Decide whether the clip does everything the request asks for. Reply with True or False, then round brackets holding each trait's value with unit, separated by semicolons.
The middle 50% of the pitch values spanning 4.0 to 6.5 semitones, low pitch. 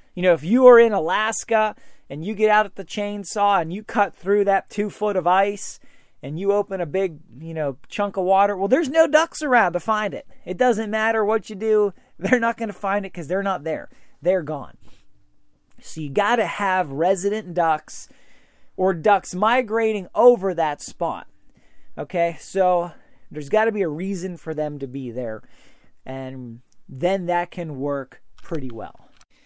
False (4.7 semitones; 195 Hz)